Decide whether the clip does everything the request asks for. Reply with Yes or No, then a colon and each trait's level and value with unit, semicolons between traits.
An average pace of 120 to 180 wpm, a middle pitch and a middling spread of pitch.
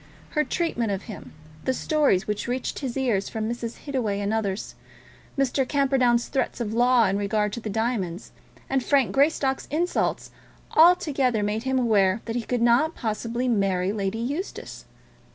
No: average, 160 wpm; high, 235 Hz; average, 4.2 semitones